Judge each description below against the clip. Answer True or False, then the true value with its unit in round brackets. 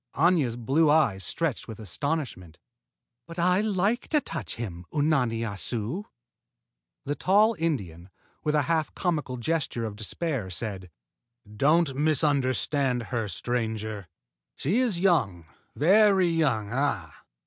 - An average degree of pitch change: False (7.1 semitones)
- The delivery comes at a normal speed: False (120 wpm)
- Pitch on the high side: False (140 Hz)